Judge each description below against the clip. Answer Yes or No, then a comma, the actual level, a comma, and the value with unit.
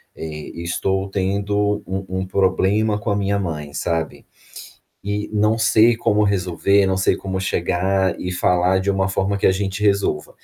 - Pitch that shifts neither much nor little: No, narrow, 1.7 semitones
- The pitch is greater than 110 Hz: No, very low, 95 Hz